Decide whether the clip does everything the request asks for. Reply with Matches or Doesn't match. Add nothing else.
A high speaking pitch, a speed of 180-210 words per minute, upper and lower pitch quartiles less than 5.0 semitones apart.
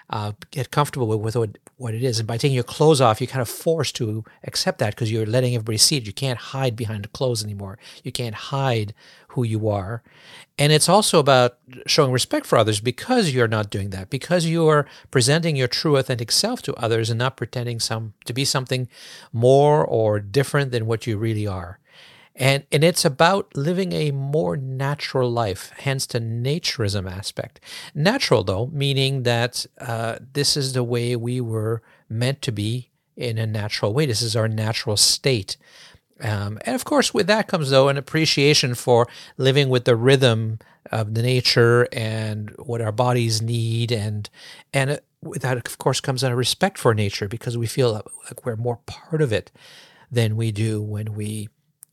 Doesn't match